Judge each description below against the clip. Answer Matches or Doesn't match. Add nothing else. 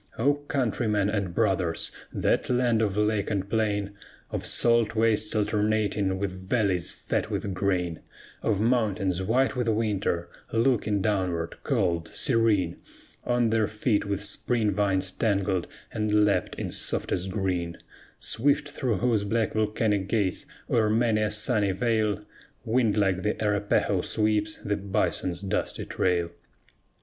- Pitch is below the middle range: Matches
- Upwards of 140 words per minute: Doesn't match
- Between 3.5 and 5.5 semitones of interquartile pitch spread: Doesn't match